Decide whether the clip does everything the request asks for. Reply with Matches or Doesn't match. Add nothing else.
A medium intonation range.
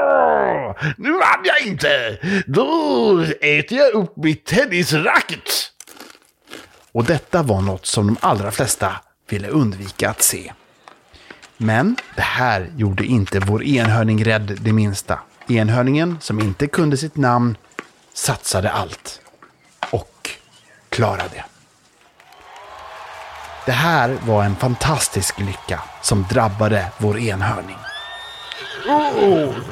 Doesn't match